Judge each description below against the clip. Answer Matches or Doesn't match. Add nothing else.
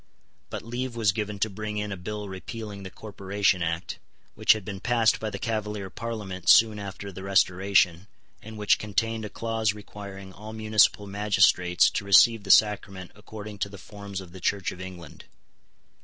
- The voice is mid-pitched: Doesn't match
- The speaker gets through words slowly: Doesn't match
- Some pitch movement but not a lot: Doesn't match